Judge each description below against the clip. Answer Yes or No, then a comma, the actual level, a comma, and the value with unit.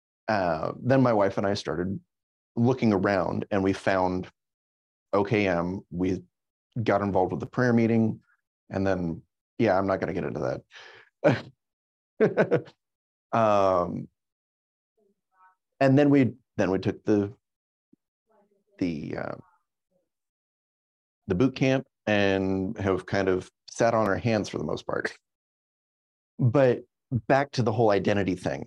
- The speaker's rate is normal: No, slow, 130 wpm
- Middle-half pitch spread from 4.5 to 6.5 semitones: Yes, average, 5.3 semitones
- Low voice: Yes, low, 100 Hz